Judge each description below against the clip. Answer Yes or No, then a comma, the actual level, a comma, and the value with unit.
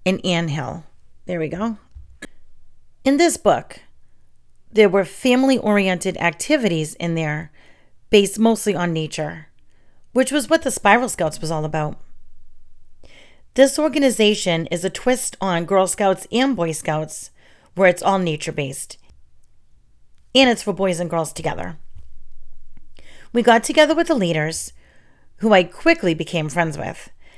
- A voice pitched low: No, medium, 185 Hz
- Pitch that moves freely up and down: Yes, wide, 6.0 semitones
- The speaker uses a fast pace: No, slow, 135 wpm